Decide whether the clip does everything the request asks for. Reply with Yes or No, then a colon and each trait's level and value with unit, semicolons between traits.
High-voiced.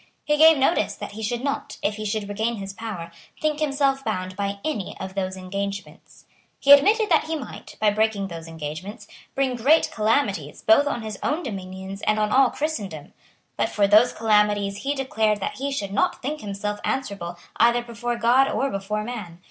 Yes: high, 215 Hz